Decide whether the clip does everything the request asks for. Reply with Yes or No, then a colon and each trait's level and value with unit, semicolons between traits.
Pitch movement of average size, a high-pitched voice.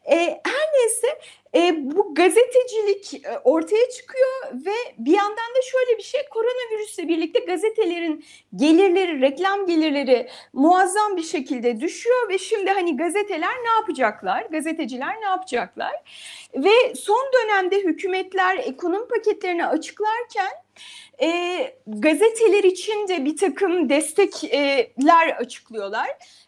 No: wide, 5.7 semitones; very high, 375 Hz